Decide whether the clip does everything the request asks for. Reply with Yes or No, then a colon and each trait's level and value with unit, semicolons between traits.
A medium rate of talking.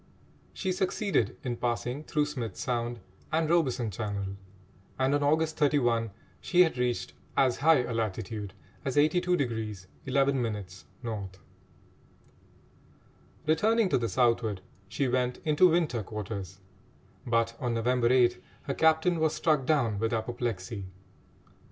No: slow, 125 wpm